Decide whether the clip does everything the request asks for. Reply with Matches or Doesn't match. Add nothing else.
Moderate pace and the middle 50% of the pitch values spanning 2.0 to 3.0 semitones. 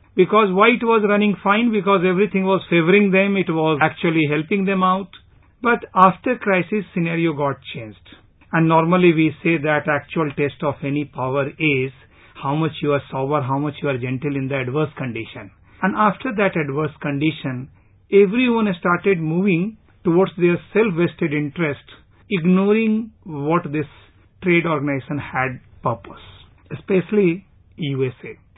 Doesn't match